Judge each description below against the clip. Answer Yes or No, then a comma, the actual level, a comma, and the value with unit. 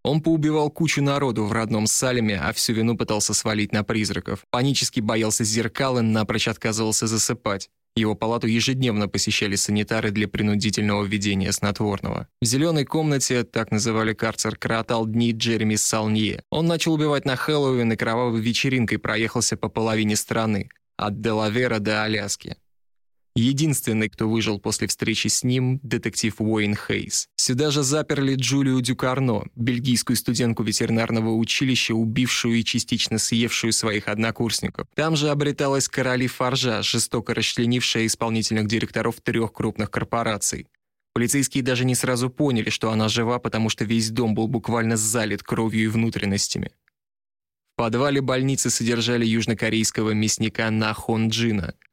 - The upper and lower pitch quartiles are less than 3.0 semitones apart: Yes, narrow, 2.5 semitones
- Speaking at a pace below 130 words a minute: No, average, 140 wpm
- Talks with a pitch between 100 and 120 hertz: Yes, low, 115 Hz